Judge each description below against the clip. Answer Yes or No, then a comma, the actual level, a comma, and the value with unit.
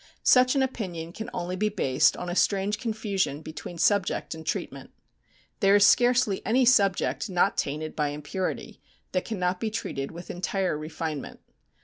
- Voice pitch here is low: No, medium, 185 Hz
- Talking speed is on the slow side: No, average, 155 wpm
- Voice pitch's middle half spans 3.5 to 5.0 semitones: Yes, average, 4.6 semitones